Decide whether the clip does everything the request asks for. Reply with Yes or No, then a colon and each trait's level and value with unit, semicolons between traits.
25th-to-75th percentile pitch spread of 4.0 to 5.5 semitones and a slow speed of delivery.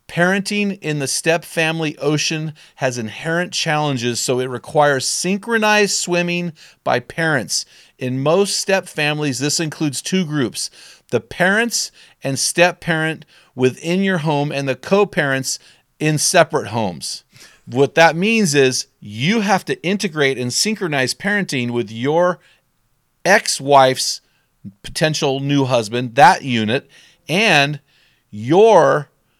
Yes: average, 4.8 semitones; slow, 125 wpm